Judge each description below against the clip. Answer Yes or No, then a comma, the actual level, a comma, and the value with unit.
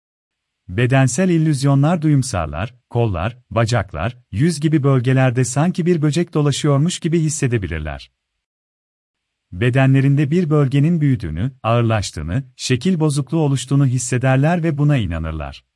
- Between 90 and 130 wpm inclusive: Yes, average, 100 wpm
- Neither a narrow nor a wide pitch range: No, wide, 8.1 semitones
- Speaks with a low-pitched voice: Yes, low, 130 Hz